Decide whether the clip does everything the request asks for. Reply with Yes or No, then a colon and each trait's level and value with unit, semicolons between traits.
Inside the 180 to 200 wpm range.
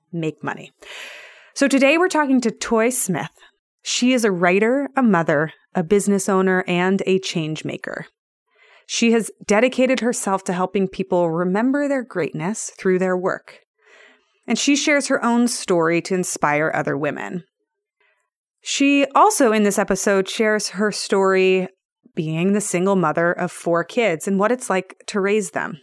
No: average, 155 wpm